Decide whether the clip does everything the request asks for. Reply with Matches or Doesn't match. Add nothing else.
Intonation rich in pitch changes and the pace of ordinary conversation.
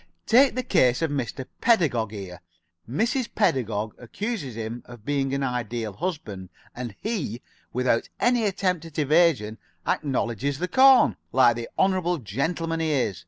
Matches